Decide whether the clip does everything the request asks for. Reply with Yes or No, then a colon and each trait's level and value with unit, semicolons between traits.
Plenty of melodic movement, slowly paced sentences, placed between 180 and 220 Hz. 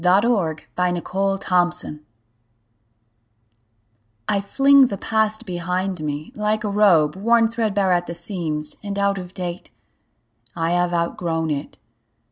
No: average, 3.4 semitones; slow, 130 wpm; medium, 185 Hz